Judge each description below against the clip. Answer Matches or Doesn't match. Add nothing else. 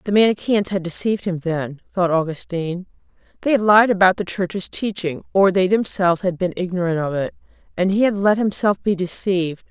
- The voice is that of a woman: Matches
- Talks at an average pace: Matches